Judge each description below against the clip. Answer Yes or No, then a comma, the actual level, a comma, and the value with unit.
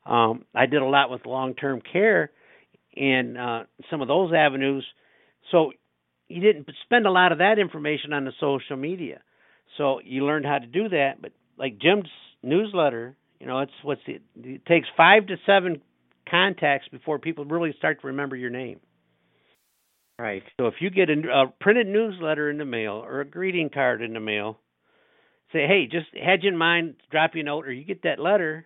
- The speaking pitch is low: No, medium, 145 Hz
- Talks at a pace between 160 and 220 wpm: Yes, average, 195 wpm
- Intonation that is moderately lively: Yes, average, 4.8 semitones